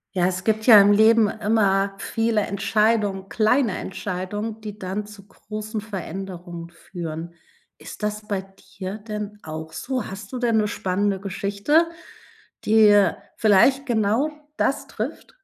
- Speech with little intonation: Yes, narrow, 2.3 semitones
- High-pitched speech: Yes, high, 205 Hz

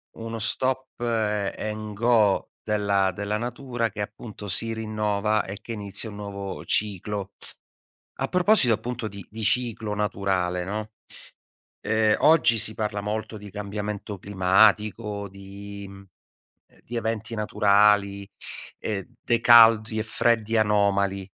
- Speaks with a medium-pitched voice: No, low, 105 Hz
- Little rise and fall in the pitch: Yes, narrow, 1.9 semitones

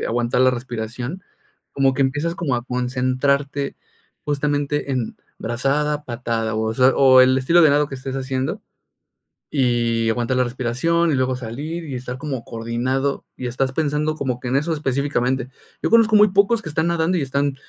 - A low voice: Yes, low, 130 Hz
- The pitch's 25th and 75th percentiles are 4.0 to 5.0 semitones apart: No, average, 3.0 semitones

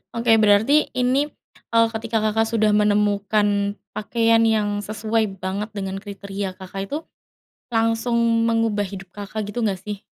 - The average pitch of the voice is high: Yes, high, 215 Hz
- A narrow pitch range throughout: Yes, narrow, 1.9 semitones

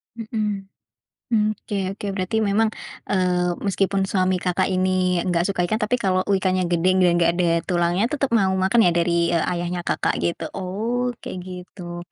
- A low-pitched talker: No, medium, 185 Hz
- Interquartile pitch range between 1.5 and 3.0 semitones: Yes, narrow, 2.4 semitones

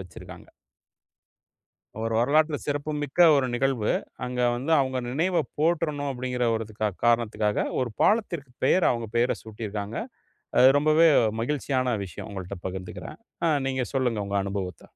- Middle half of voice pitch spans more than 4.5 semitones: Yes, average, 5.0 semitones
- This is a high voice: No, low, 125 Hz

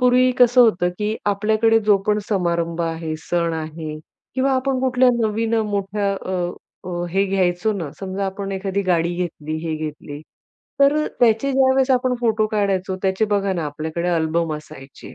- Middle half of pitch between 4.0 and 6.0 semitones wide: Yes, average, 4.9 semitones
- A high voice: Yes, high, 195 Hz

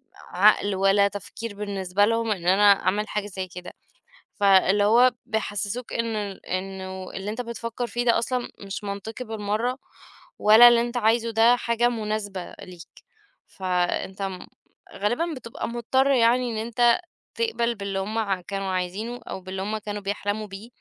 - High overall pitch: Yes, high, 210 Hz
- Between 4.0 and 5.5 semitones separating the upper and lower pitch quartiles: No, average, 3.2 semitones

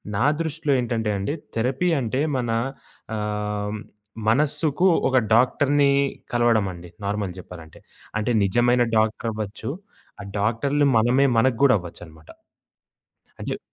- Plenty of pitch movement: No, average, 4.1 semitones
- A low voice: Yes, low, 115 Hz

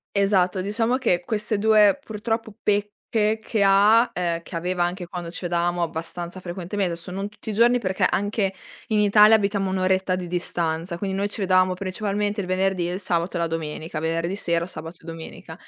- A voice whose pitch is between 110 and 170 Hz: No, high, 190 Hz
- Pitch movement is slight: No, average, 3.0 semitones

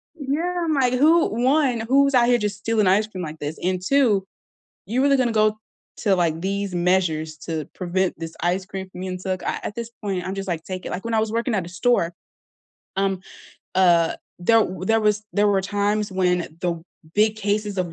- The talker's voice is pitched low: No, high, 200 Hz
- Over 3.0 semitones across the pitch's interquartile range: Yes, average, 3.8 semitones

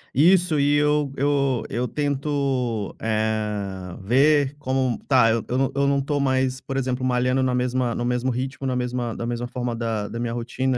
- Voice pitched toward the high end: No, low, 130 Hz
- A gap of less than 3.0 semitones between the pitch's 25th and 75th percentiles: Yes, narrow, 2.6 semitones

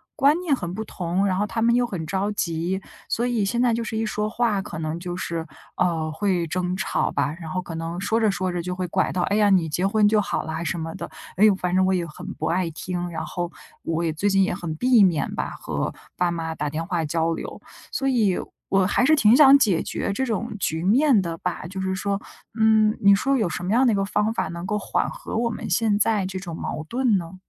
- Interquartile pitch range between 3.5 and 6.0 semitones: Yes, average, 4.1 semitones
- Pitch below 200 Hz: Yes, high, 190 Hz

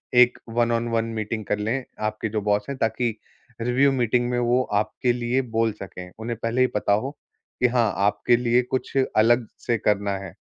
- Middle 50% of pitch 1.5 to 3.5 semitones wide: Yes, narrow, 2.5 semitones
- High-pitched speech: No, low, 115 Hz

